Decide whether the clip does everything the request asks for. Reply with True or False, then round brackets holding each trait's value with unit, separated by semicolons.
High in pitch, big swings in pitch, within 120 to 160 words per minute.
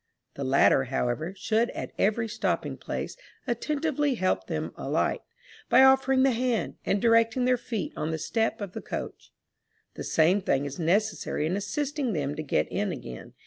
False (210 Hz; 7.9 semitones; 170 wpm)